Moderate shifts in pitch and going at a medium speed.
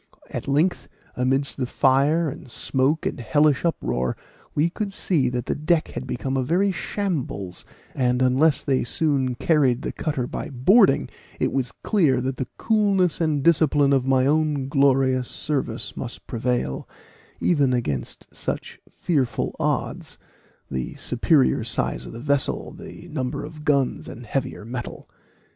Yes: average, 3.7 semitones; average, 150 wpm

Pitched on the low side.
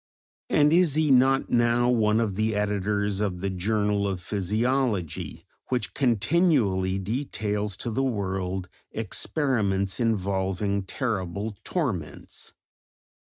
Yes: low, 105 Hz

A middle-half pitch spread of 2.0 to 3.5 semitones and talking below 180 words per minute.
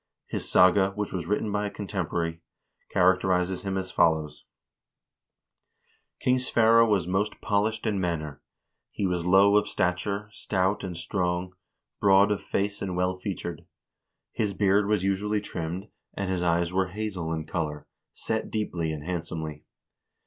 Yes: average, 2.8 semitones; average, 150 wpm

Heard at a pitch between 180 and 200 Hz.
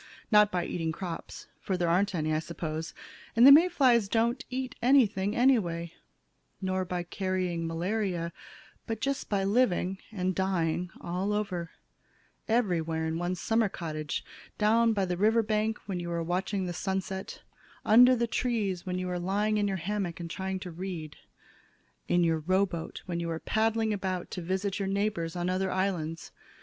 Yes: high, 190 Hz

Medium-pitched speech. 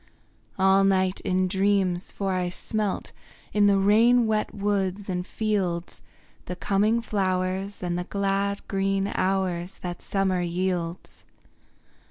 No: high, 195 Hz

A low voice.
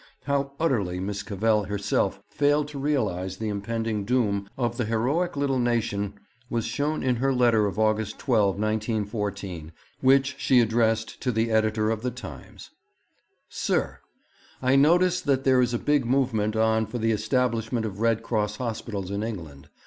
Yes: low, 115 Hz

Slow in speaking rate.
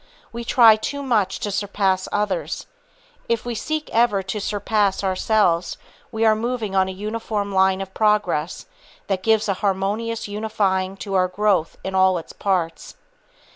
No: average, 155 wpm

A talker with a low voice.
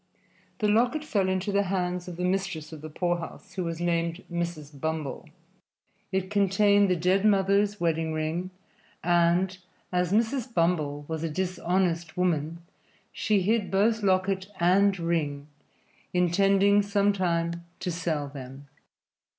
No: medium, 180 Hz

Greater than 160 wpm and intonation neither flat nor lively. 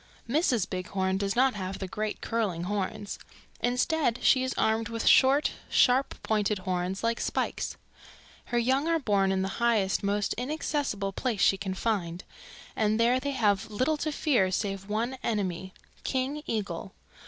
No: average, 155 wpm; average, 4.7 semitones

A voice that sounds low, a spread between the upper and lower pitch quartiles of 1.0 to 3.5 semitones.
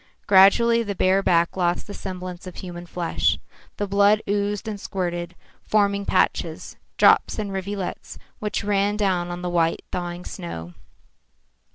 No: high, 190 Hz; narrow, 2.5 semitones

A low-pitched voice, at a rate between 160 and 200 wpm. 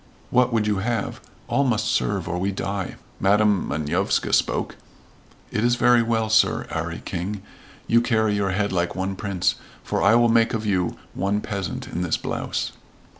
Yes: low, 105 Hz; average, 170 wpm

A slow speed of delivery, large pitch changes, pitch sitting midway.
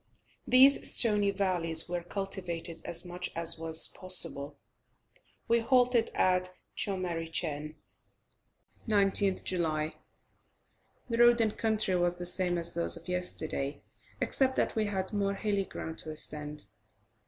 No: slow, 125 wpm; average, 3.7 semitones; medium, 180 Hz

